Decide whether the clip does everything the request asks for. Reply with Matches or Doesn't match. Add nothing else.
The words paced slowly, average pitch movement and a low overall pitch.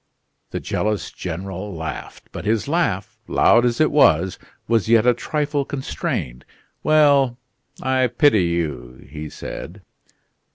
Doesn't match